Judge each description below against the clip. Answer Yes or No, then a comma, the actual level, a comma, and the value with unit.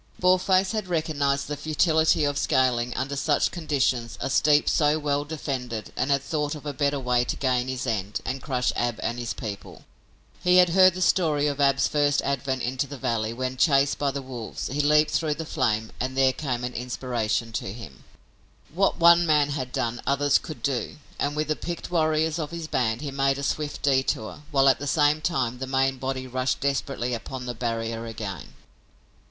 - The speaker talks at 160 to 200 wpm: Yes, average, 195 wpm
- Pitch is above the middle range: No, medium, 140 Hz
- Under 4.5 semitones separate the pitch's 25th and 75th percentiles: Yes, average, 3.3 semitones